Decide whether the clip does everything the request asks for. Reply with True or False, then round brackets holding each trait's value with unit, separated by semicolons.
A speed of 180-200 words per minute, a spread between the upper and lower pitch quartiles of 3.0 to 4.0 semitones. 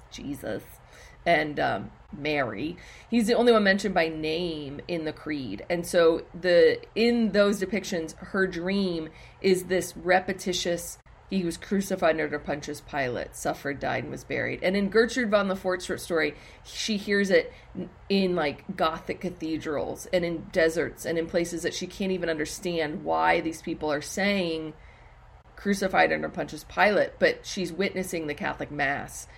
False (155 wpm; 3.3 semitones)